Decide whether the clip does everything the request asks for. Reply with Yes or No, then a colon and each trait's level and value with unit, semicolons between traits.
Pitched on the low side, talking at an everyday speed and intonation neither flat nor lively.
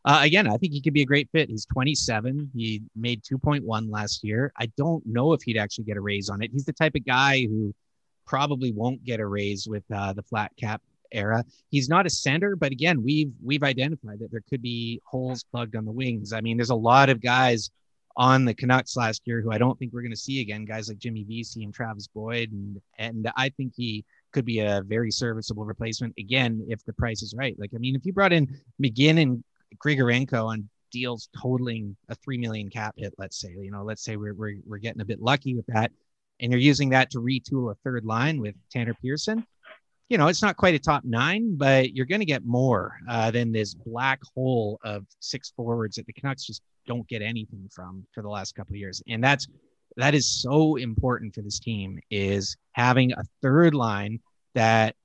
No: low, 120 Hz; fast, 220 wpm; average, 3.6 semitones